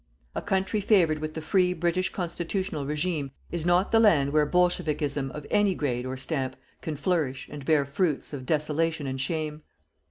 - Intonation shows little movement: No, average, 3.9 semitones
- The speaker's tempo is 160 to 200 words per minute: Yes, average, 170 wpm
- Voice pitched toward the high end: No, medium, 155 Hz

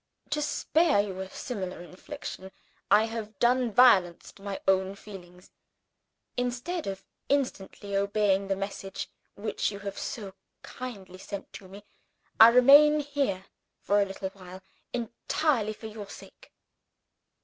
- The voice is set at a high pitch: Yes, high, 205 Hz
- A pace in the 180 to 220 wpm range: No, slow, 135 wpm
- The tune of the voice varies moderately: Yes, average, 4.3 semitones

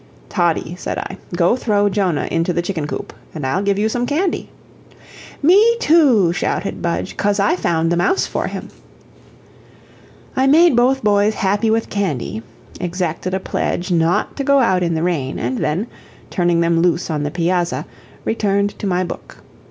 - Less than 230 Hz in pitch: Yes, medium, 185 Hz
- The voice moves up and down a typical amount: Yes, average, 4.3 semitones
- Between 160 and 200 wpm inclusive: Yes, average, 170 wpm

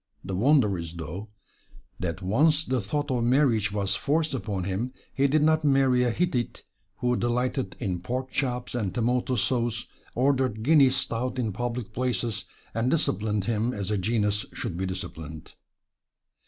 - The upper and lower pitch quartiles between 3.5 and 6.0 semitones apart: Yes, average, 4.3 semitones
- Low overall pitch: Yes, low, 120 Hz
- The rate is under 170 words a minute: Yes, average, 155 wpm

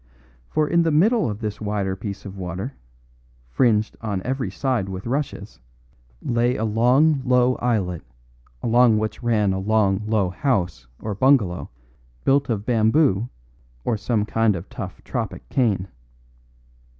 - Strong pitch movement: No, average, 4.3 semitones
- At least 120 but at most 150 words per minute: Yes, average, 140 wpm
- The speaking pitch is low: Yes, low, 110 Hz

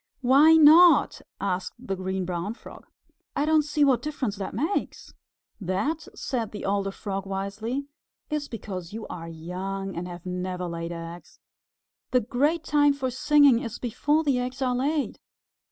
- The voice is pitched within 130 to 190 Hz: No, high, 225 Hz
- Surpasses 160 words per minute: No, average, 155 wpm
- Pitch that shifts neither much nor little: No, wide, 7.3 semitones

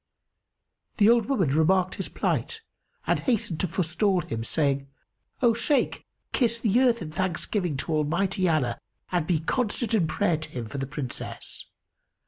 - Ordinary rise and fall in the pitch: No, wide, 6.0 semitones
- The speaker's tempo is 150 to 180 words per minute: Yes, average, 155 wpm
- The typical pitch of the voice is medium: Yes, medium, 175 Hz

